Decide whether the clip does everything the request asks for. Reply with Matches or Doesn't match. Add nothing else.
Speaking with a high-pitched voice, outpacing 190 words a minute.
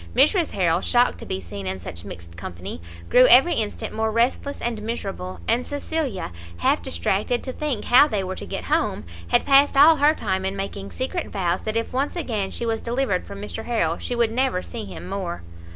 Matches